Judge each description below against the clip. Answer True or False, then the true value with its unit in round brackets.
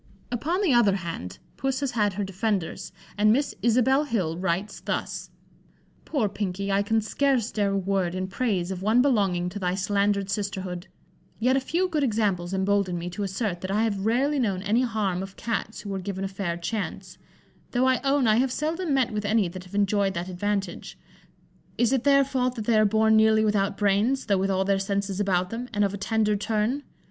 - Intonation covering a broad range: False (3.6 semitones)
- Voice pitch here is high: True (205 Hz)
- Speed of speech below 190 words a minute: False (205 wpm)